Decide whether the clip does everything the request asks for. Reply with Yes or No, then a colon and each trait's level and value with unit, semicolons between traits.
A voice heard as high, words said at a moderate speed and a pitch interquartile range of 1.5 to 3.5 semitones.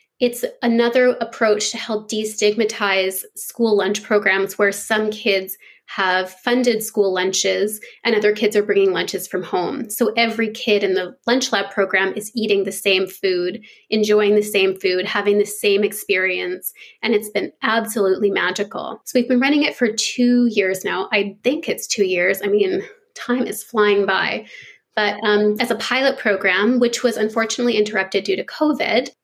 Yes: high, 210 Hz; average, 170 wpm; average, 2.8 semitones